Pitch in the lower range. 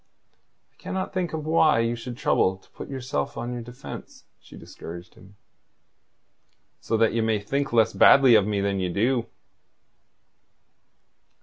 Yes: low, 115 Hz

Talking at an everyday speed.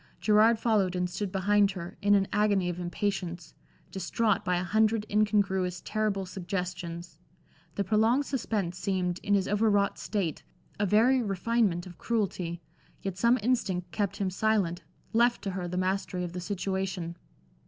Yes: average, 155 wpm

